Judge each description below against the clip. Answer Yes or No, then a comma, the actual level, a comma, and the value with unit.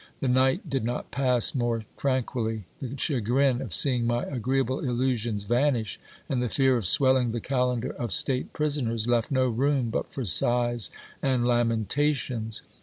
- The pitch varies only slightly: Yes, narrow, 2.3 semitones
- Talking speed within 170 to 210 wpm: No, average, 155 wpm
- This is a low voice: Yes, low, 125 Hz